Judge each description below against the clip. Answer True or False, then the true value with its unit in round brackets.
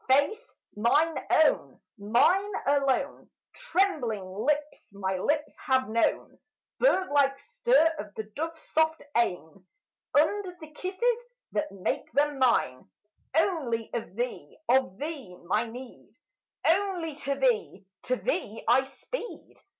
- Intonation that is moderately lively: False (6.0 semitones)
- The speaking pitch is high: True (280 Hz)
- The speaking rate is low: True (120 wpm)